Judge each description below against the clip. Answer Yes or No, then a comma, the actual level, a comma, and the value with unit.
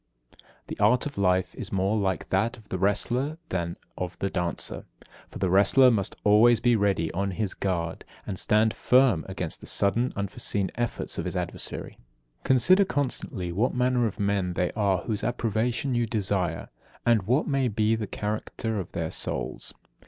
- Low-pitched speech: Yes, low, 105 Hz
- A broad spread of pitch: No, average, 4.2 semitones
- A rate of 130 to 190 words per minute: Yes, average, 175 wpm